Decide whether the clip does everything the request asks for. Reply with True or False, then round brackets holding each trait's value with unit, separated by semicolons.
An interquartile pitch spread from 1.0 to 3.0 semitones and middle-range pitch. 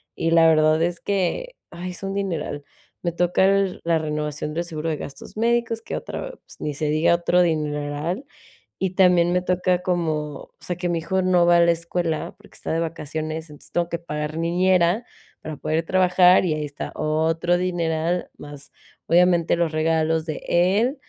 True (2.4 semitones; 170 Hz)